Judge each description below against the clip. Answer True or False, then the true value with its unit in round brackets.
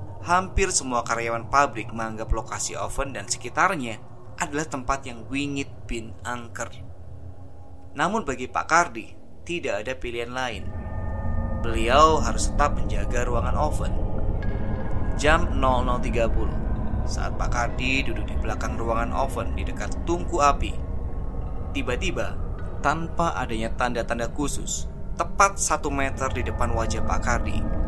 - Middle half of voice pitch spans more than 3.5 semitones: True (5.1 semitones)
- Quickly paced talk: False (120 wpm)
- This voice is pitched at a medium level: False (110 Hz)